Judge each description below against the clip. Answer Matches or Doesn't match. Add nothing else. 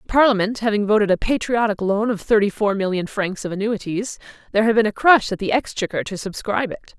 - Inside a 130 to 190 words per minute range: Doesn't match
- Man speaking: Doesn't match